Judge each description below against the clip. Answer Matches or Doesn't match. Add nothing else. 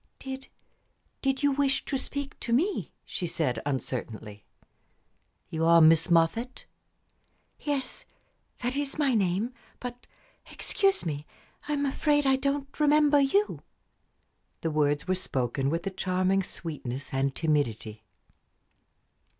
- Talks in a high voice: Matches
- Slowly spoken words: Matches